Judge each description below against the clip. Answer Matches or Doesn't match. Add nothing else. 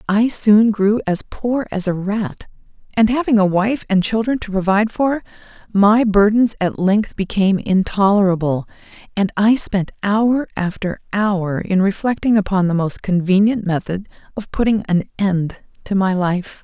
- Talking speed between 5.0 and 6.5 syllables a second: Doesn't match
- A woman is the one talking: Matches